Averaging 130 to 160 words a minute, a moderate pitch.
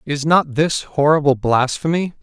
Yes: slow, 135 wpm; medium, 150 Hz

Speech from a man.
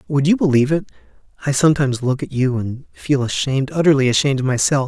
Yes: male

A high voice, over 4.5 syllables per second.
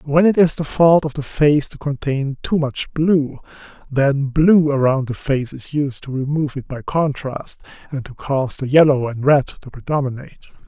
No: medium, 140 Hz; 4.8 syllables/s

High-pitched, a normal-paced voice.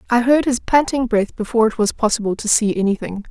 No: high, 225 Hz; fast, 220 wpm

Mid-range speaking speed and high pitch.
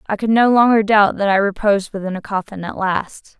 No: fast, 230 wpm; high, 205 Hz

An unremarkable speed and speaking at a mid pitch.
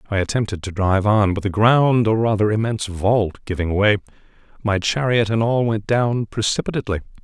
No: average, 175 wpm; low, 105 Hz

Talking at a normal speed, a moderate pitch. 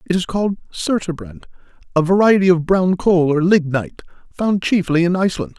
Yes: average, 160 wpm; medium, 175 Hz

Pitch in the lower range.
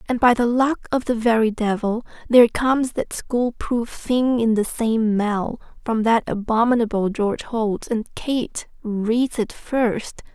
No: high, 230 Hz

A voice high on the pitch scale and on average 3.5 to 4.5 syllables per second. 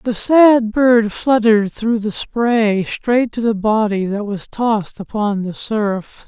Yes: high, 220 Hz; 3.6 syllables/s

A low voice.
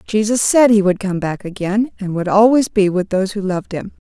No: high, 200 Hz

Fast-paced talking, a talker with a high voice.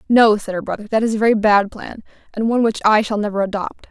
Yes: fast, 260 wpm; high, 215 Hz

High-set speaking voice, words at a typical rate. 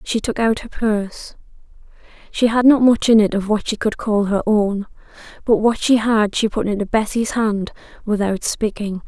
Yes: high, 215 Hz; average, 190 wpm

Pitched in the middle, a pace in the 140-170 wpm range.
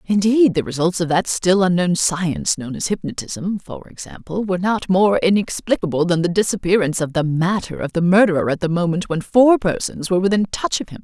No: medium, 180 Hz; average, 200 wpm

